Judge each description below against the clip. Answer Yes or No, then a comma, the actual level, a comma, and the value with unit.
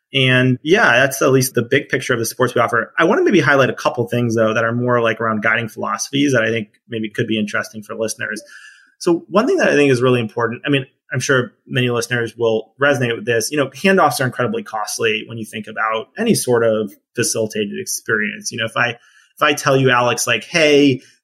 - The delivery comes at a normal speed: No, fast, 235 wpm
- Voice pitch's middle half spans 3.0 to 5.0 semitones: Yes, average, 3.7 semitones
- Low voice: Yes, low, 125 Hz